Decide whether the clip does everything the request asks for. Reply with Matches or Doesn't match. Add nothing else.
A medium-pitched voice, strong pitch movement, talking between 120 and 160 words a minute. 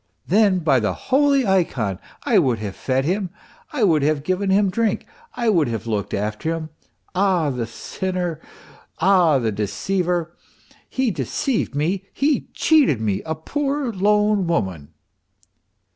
Matches